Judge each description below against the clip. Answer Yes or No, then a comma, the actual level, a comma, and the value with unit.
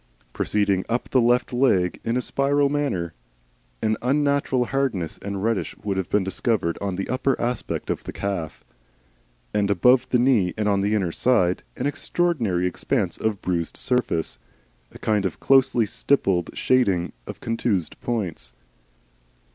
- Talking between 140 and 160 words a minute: Yes, average, 150 wpm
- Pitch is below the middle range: Yes, low, 110 Hz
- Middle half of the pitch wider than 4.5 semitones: Yes, average, 5.2 semitones